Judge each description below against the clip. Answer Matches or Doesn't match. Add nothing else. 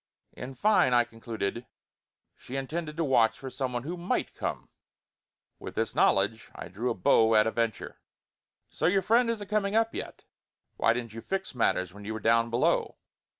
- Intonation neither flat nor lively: Doesn't match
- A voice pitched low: Matches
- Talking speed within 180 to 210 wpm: Matches